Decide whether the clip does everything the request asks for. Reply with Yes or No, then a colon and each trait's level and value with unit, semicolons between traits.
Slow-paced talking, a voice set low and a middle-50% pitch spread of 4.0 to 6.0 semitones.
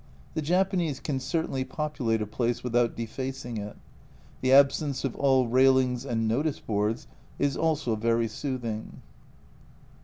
No: slow, 130 wpm; low, 130 Hz; average, 3.6 semitones